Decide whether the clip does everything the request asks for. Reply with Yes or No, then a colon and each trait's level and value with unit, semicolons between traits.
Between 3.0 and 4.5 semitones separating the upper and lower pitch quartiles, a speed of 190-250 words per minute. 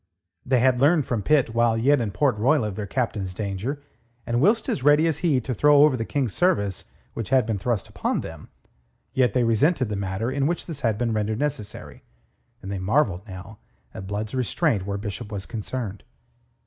No: average, 5.2 semitones; average, 200 wpm